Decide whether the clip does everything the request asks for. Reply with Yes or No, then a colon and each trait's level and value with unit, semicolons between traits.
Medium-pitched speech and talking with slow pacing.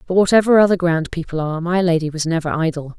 No: medium, 170 Hz; fast, 220 wpm